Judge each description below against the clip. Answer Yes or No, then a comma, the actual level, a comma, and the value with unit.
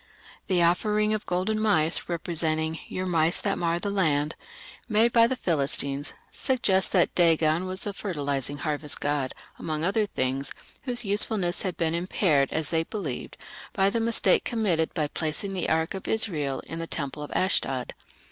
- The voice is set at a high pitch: No, medium, 170 Hz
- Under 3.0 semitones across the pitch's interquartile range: No, average, 4.6 semitones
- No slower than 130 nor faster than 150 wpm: No, average, 165 wpm